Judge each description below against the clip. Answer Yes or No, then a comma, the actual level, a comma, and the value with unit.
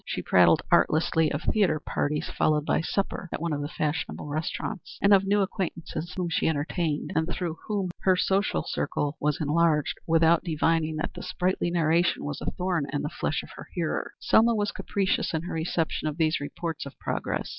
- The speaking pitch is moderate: Yes, medium, 165 Hz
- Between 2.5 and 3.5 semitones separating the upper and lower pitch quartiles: Yes, average, 2.9 semitones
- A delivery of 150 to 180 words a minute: No, average, 195 wpm